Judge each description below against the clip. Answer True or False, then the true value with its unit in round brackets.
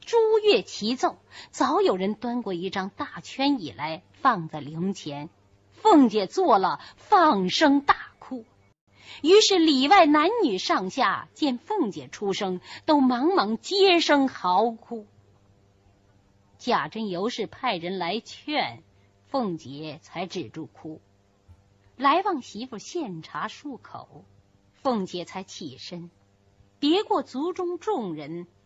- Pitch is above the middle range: True (215 Hz)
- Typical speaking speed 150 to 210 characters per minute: True (165 characters per minute)